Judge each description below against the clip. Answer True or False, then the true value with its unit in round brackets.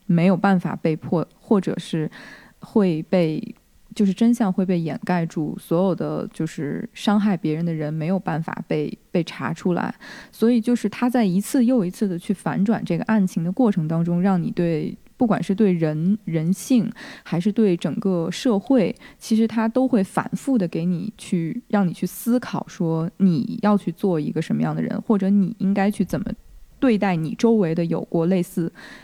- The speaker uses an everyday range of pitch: True (4.2 semitones)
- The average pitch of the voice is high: True (195 Hz)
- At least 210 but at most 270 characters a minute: True (260 characters per minute)